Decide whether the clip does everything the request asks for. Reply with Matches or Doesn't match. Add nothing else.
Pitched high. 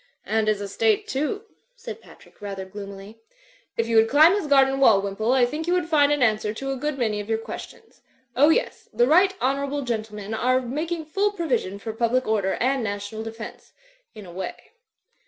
Matches